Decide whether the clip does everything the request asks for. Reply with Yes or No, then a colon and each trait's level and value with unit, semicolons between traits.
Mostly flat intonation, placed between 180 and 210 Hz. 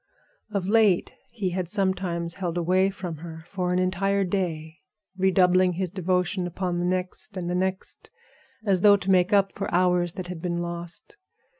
Yes: narrow, 1.6 semitones; medium, 185 Hz